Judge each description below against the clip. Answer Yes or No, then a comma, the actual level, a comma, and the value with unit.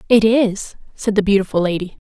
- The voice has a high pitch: Yes, high, 205 Hz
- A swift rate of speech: No, average, 175 wpm